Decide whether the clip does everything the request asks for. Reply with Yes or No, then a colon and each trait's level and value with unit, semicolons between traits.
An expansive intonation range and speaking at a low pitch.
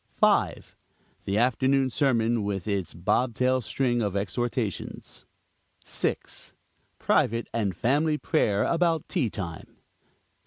No: average, 4.6 semitones; low, 115 Hz